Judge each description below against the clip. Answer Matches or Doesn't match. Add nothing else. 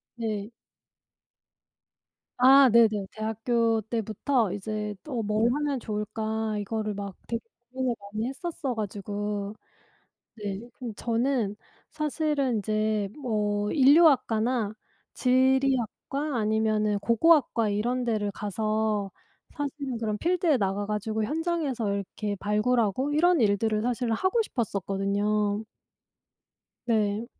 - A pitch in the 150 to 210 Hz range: Doesn't match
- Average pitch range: Matches